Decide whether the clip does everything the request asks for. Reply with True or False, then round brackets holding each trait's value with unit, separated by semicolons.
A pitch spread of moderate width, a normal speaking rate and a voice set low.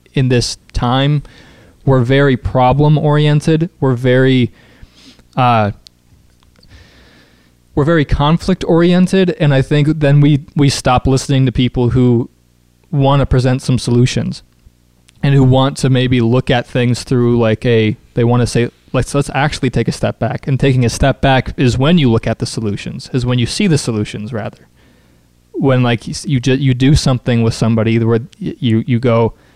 True (3.2 semitones; 170 wpm; 125 Hz)